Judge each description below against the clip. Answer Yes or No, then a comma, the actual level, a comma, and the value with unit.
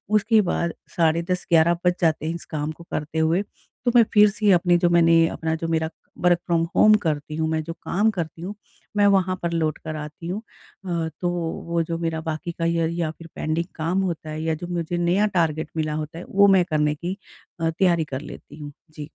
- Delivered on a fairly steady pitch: Yes, narrow, 1.8 semitones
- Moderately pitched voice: Yes, medium, 165 Hz